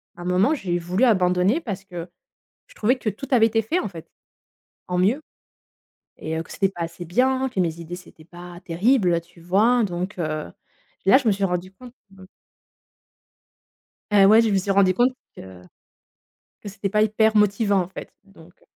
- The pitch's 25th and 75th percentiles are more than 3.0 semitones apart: Yes, average, 3.8 semitones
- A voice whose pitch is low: No, high, 195 Hz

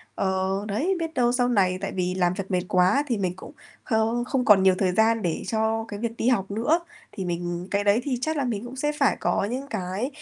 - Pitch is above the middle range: Yes, high, 215 Hz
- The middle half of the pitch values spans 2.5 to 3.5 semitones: No, average, 4.6 semitones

